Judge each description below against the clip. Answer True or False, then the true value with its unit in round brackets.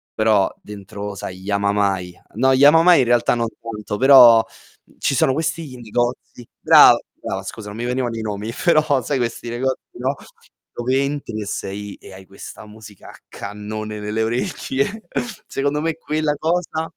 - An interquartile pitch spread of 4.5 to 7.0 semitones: True (4.9 semitones)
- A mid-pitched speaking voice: False (115 Hz)